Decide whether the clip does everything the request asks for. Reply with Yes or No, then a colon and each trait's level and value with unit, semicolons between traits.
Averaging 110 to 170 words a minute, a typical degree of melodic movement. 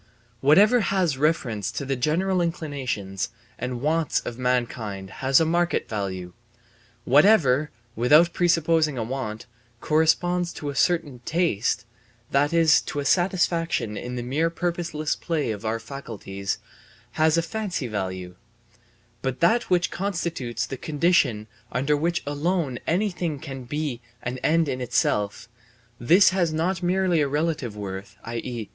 No: average, 140 wpm; wide, 5.8 semitones